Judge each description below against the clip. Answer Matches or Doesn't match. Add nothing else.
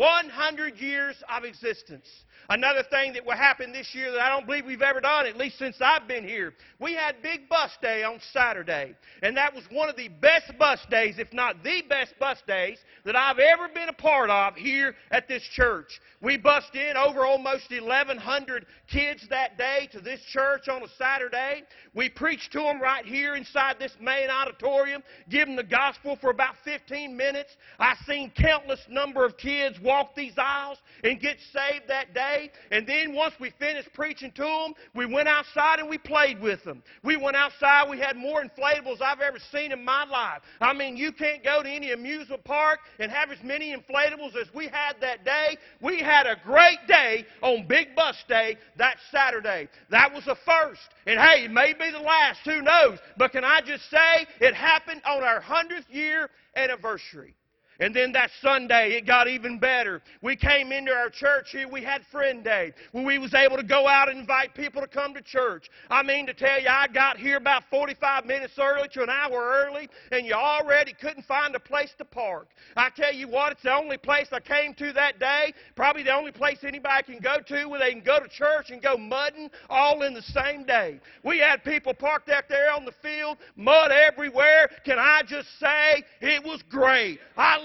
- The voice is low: Doesn't match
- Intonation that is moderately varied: Doesn't match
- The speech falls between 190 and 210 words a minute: Matches